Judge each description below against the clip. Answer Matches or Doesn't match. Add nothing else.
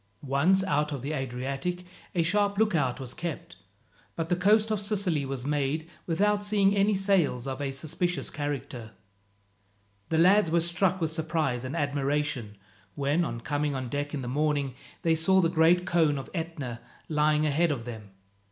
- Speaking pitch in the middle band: Matches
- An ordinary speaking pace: Matches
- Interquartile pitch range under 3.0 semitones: Doesn't match